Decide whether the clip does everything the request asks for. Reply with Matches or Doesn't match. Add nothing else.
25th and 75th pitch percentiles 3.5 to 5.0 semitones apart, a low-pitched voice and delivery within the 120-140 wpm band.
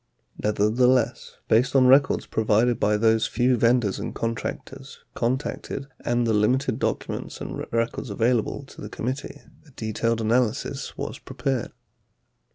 Doesn't match